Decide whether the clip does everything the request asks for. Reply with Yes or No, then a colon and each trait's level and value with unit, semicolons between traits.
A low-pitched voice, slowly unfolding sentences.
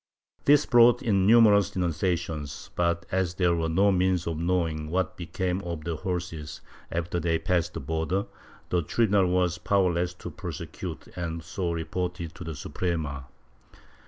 No: very low, 90 Hz; average, 150 wpm